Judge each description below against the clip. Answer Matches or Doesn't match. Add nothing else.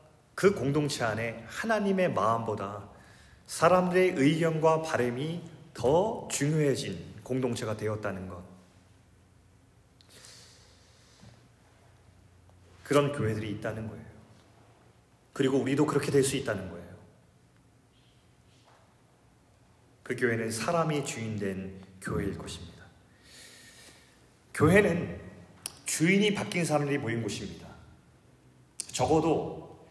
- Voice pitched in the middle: Doesn't match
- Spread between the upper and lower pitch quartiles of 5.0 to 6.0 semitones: Doesn't match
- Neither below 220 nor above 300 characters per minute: Doesn't match